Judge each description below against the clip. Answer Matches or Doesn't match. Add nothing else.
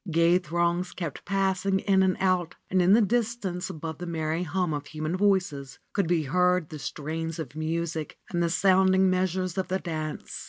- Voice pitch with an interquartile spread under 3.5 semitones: Matches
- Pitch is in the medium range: Matches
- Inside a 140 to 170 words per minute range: Doesn't match